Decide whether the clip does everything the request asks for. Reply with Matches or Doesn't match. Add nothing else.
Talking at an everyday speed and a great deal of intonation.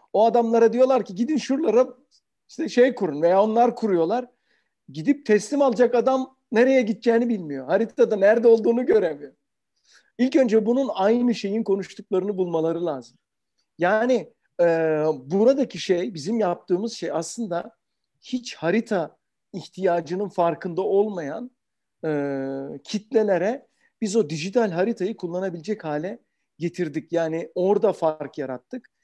Matches